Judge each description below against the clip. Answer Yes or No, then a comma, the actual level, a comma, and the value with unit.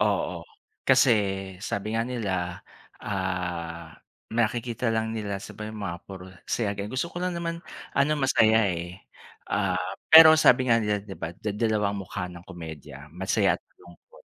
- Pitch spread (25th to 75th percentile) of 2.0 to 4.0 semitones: No, average, 4.4 semitones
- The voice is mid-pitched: No, low, 105 Hz